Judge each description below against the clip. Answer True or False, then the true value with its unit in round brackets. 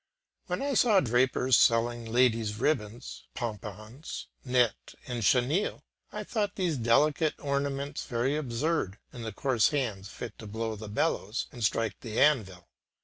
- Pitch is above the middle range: False (120 Hz)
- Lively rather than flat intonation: False (4.3 semitones)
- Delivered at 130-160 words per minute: True (145 wpm)